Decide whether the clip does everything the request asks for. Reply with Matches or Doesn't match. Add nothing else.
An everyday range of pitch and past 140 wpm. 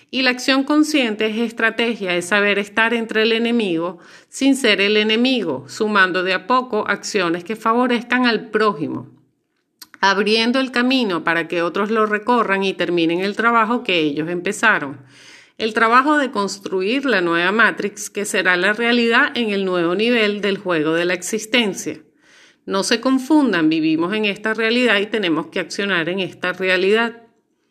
Matches